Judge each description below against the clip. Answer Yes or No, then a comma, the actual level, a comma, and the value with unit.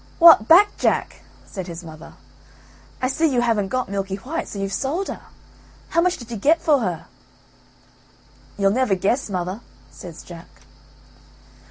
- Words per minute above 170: No, average, 155 wpm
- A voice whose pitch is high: Yes, high, 215 Hz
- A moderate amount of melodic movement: No, wide, 6.6 semitones